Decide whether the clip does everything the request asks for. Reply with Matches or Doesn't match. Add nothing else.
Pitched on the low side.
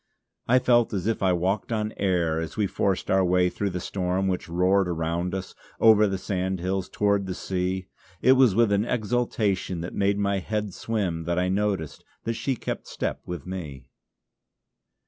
Matches